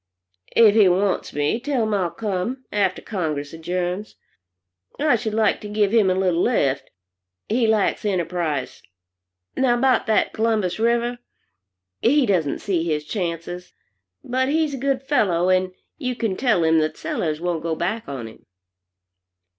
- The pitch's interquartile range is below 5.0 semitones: No, wide, 5.4 semitones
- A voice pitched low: No, high, 200 Hz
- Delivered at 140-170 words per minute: Yes, average, 155 wpm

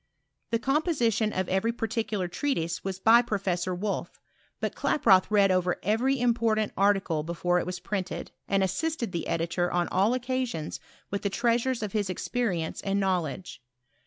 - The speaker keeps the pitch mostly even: No, average, 4.2 semitones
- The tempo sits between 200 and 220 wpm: No, average, 160 wpm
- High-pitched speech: Yes, high, 200 Hz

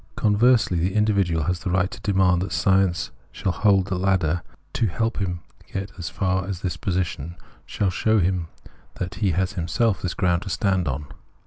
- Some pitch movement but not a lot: No, narrow, 2.1 semitones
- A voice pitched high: No, very low, 95 Hz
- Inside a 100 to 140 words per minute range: No, fast, 205 wpm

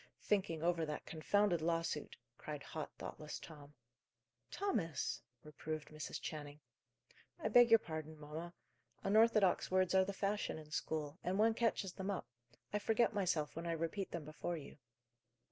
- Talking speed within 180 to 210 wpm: No, average, 150 wpm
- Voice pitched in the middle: Yes, medium, 170 Hz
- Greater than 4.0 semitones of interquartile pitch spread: Yes, average, 4.4 semitones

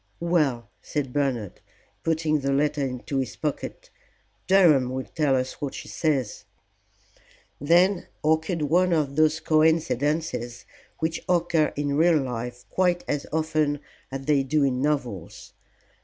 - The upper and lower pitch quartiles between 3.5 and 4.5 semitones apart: No, average, 3.1 semitones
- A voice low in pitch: No, medium, 150 Hz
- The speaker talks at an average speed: No, slow, 130 wpm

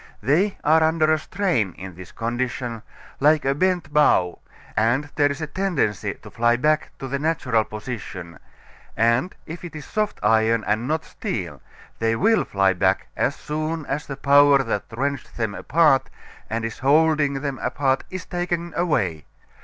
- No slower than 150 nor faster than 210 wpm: Yes, average, 165 wpm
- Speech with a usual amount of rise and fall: No, wide, 5.7 semitones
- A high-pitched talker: No, medium, 140 Hz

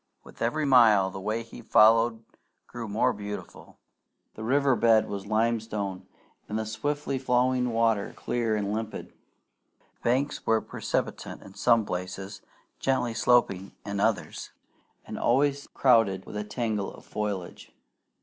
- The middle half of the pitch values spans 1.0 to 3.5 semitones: Yes, average, 3.0 semitones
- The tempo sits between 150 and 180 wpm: No, average, 140 wpm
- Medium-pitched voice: No, low, 110 Hz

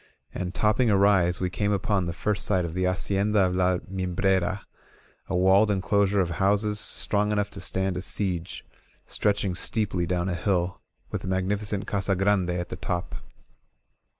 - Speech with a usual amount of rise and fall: No, narrow, 2.1 semitones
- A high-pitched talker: No, very low, 95 Hz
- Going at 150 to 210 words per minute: Yes, average, 170 wpm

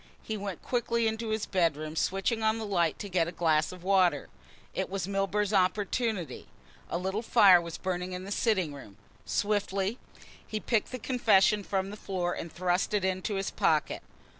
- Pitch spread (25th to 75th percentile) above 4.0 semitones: No, average, 3.1 semitones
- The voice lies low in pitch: No, high, 195 Hz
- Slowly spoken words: No, average, 180 wpm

